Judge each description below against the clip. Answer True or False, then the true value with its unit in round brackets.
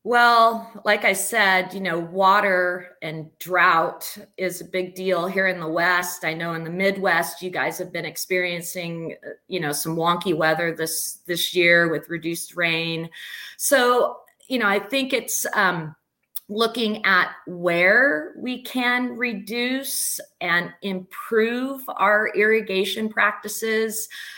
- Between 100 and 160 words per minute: True (140 wpm)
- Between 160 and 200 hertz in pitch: True (185 Hz)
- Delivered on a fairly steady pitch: False (4.4 semitones)